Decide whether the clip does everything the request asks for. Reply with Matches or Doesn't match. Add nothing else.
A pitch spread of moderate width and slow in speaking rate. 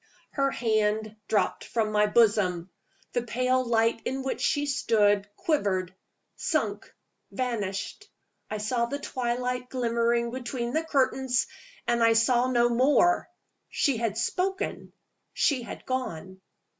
Matches